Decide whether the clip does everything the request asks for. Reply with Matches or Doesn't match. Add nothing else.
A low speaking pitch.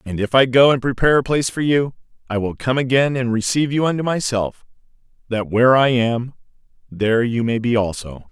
Matches